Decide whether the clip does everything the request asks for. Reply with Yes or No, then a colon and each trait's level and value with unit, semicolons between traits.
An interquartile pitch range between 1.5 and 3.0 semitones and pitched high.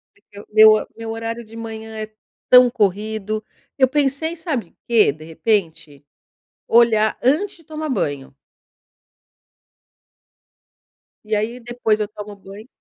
Yes: average, 2.7 semitones; high, 220 Hz